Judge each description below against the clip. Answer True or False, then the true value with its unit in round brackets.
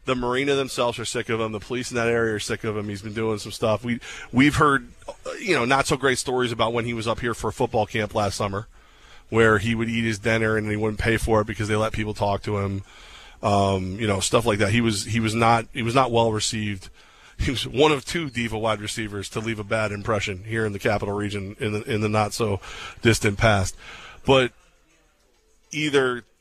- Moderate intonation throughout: False (2.0 semitones)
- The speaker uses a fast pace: True (240 wpm)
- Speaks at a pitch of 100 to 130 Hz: True (110 Hz)